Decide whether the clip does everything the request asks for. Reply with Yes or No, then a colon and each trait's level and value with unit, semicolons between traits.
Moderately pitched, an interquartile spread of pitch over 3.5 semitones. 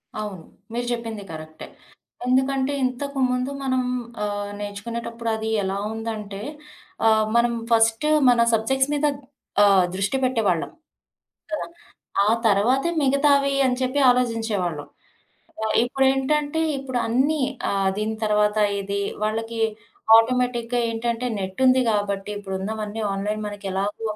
No: high, 225 Hz; average, 3.9 semitones